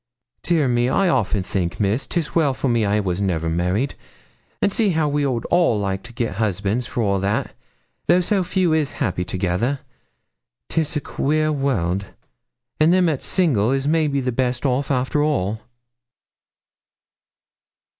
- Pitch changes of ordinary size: No, wide, 7.3 semitones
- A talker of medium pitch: No, low, 125 Hz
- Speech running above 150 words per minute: Yes, average, 160 wpm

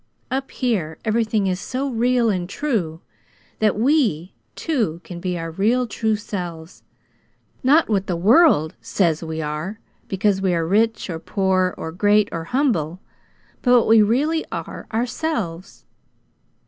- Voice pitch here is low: No, high, 205 Hz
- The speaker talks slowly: No, average, 145 wpm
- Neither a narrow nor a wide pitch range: No, wide, 5.7 semitones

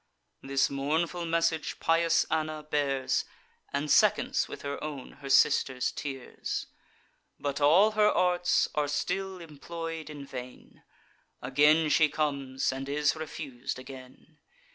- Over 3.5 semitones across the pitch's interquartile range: No, average, 3.1 semitones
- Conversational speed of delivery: No, slow, 120 wpm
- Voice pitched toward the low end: No, medium, 150 Hz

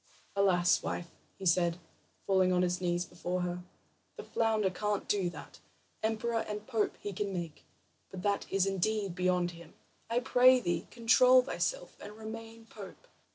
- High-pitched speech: Yes, high, 195 Hz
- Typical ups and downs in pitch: Yes, average, 3.8 semitones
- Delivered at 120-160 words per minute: Yes, average, 155 wpm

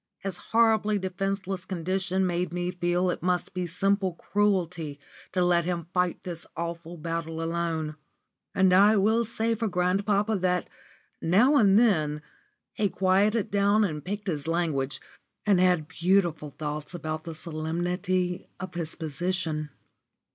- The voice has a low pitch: No, medium, 180 Hz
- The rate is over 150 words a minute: No, average, 140 wpm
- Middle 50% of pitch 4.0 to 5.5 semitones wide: No, average, 2.9 semitones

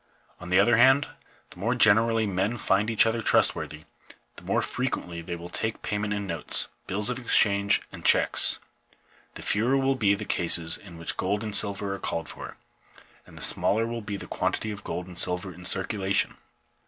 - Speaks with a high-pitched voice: No, low, 100 Hz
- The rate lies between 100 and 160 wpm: No, average, 190 wpm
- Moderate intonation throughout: Yes, average, 3.6 semitones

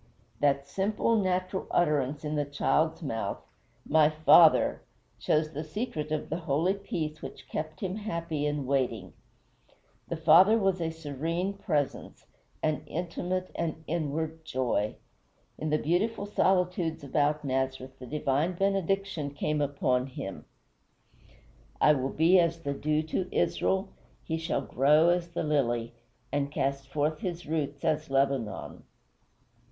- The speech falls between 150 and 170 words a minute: No, slow, 135 wpm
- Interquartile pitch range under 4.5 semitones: Yes, average, 3.6 semitones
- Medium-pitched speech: Yes, medium, 155 Hz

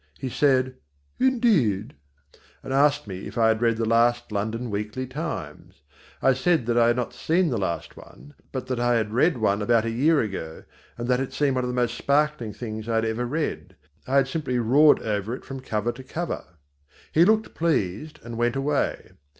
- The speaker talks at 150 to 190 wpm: No, average, 200 wpm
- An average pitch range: Yes, average, 4.1 semitones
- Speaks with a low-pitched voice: Yes, low, 120 Hz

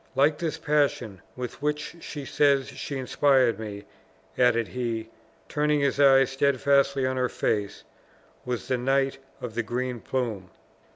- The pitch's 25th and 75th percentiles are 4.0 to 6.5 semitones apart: No, average, 2.8 semitones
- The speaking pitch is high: No, low, 130 Hz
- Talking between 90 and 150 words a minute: Yes, average, 140 wpm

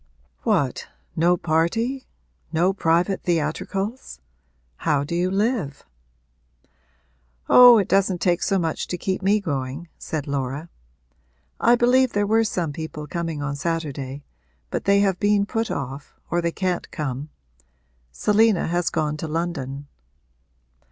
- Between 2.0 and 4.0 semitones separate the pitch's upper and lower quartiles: No, average, 4.9 semitones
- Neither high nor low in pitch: Yes, medium, 170 Hz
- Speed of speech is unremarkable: No, slow, 130 wpm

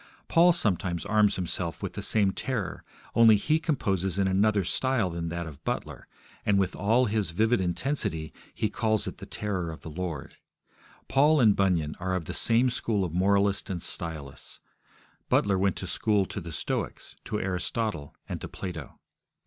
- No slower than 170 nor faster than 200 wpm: Yes, average, 175 wpm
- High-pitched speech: No, low, 100 Hz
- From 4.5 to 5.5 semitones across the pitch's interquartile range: No, average, 3.9 semitones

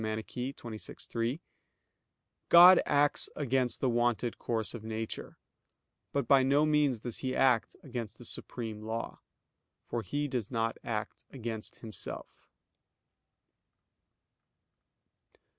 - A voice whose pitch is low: Yes, low, 120 Hz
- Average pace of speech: No, slow, 110 wpm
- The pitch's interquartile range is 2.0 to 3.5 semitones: Yes, average, 3.2 semitones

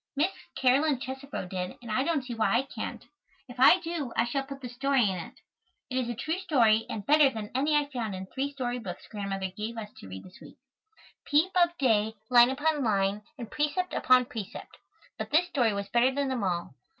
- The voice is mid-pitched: No, very high, 250 Hz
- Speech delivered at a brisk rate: Yes, fast, 215 wpm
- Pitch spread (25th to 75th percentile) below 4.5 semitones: No, average, 4.8 semitones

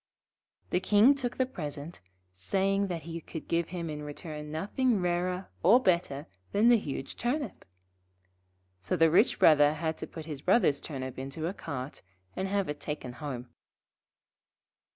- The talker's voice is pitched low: No, medium, 165 Hz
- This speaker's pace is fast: No, average, 155 wpm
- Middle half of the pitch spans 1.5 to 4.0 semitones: No, average, 4.9 semitones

